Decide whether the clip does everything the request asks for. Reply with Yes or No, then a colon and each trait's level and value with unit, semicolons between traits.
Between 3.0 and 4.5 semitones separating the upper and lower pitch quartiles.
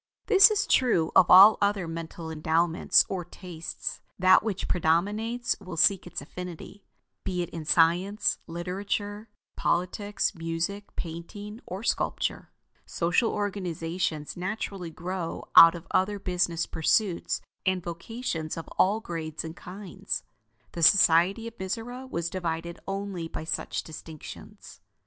Yes: average, 3.5 semitones